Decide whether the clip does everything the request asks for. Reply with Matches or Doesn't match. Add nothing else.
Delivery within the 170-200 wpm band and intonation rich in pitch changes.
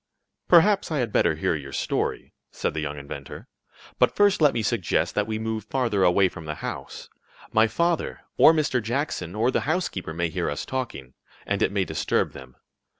Matches